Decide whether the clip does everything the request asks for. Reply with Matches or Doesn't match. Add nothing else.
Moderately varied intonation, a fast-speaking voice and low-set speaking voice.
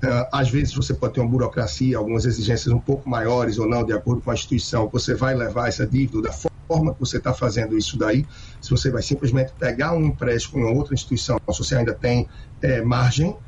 Doesn't match